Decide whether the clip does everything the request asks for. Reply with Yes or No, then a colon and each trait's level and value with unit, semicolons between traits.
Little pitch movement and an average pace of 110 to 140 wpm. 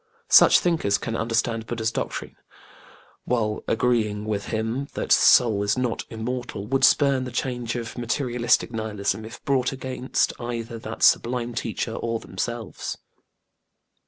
Yes: narrow, 1.9 semitones; slow, 135 wpm